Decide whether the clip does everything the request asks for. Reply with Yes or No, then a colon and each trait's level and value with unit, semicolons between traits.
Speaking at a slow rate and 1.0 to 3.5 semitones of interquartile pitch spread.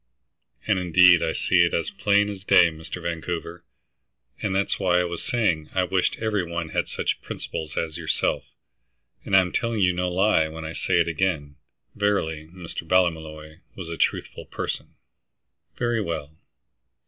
No: average, 160 wpm; average, 2.9 semitones